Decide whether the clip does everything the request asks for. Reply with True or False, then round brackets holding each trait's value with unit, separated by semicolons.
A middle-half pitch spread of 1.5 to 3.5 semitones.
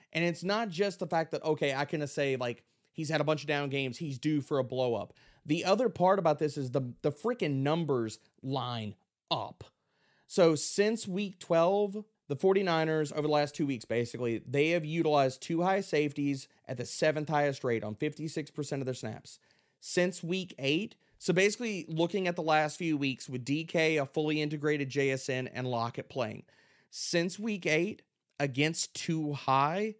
False (3.9 semitones)